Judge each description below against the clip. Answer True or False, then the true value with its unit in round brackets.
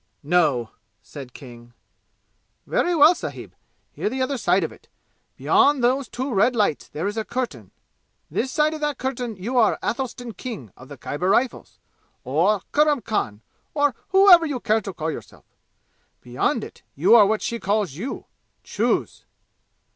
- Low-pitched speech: False (220 Hz)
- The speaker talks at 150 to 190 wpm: True (160 wpm)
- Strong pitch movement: True (8.3 semitones)